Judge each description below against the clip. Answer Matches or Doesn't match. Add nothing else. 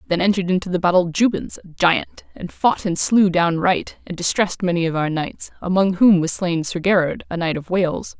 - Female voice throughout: Matches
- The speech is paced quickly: Matches